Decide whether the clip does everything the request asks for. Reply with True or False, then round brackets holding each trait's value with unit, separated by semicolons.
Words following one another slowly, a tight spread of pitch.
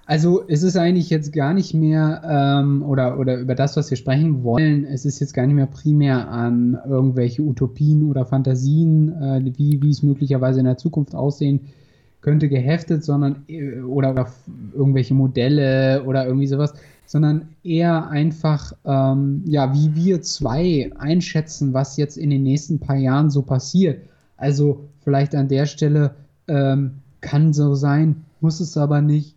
False (165 wpm; 2.2 semitones)